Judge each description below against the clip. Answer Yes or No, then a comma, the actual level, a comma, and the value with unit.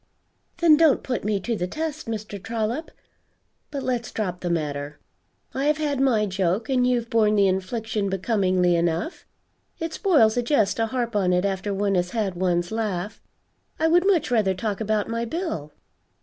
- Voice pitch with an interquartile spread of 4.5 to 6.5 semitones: Yes, average, 5.1 semitones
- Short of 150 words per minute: No, average, 175 wpm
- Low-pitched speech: No, high, 215 Hz